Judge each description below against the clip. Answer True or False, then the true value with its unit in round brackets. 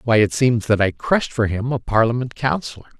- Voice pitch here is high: False (115 Hz)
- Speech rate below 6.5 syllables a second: True (5.7 syllables/s)